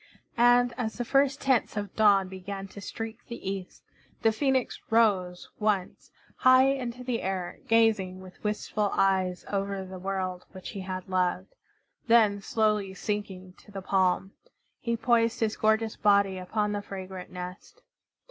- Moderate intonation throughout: Yes, average, 3.1 semitones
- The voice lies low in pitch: No, high, 200 Hz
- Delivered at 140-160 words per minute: Yes, average, 150 wpm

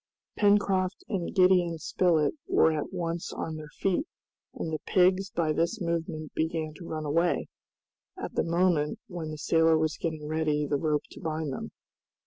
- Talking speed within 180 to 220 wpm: No, average, 165 wpm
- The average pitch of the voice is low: No, medium, 165 Hz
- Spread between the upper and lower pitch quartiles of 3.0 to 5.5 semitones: No, narrow, 2.4 semitones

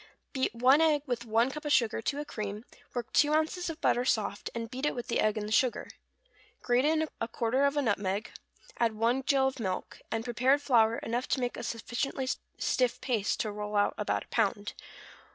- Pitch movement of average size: Yes, average, 3.6 semitones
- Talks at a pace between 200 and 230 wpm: Yes, fast, 205 wpm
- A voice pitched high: Yes, high, 245 Hz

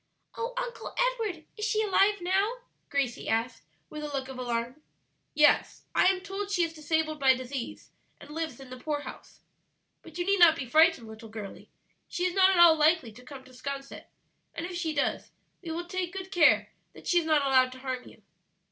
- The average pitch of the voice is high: Yes, very high, 315 Hz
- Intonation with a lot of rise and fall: Yes, wide, 5.7 semitones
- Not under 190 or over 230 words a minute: Yes, average, 200 wpm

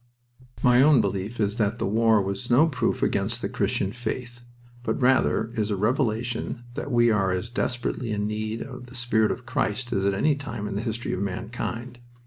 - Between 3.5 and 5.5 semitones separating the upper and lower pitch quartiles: No, average, 3.0 semitones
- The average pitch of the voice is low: Yes, low, 115 Hz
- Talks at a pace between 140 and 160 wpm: No, average, 195 wpm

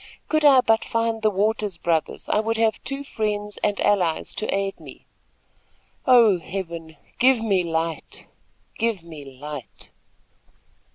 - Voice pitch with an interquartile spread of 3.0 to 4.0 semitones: No, average, 5.1 semitones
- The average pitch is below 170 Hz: No, high, 205 Hz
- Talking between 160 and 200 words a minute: No, slow, 135 wpm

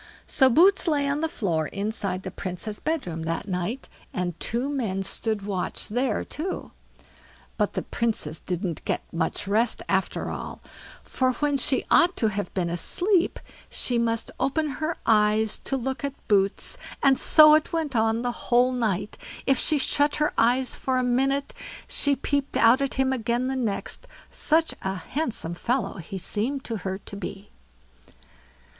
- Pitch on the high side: Yes, high, 240 Hz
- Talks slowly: No, average, 165 wpm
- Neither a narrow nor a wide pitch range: No, wide, 5.7 semitones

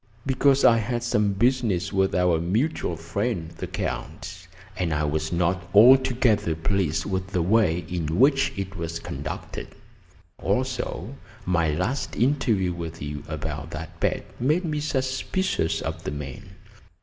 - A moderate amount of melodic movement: No, wide, 6.8 semitones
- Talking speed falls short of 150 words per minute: Yes, average, 140 wpm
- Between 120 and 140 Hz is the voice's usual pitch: No, very low, 95 Hz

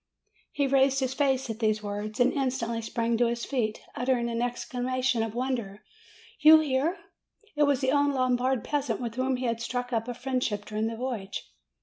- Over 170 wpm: Yes, average, 190 wpm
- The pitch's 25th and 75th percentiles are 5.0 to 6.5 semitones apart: No, narrow, 2.5 semitones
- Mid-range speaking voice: No, very high, 250 Hz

